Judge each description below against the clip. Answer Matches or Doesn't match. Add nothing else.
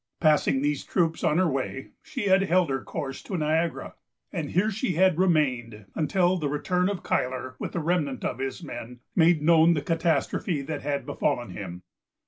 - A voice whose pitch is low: Doesn't match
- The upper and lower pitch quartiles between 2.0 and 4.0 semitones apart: Doesn't match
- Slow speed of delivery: Doesn't match